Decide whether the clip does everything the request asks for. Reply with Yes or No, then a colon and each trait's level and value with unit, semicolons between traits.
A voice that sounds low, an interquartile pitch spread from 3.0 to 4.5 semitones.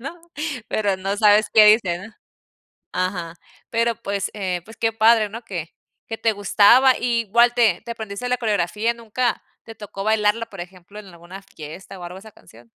No: high, 210 Hz; average, 3.3 semitones